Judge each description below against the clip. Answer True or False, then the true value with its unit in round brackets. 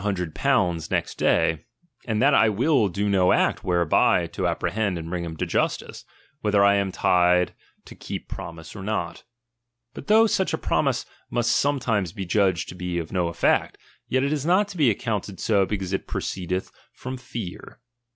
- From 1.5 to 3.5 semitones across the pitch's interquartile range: False (4.6 semitones)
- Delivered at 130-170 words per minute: False (180 wpm)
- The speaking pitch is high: False (100 Hz)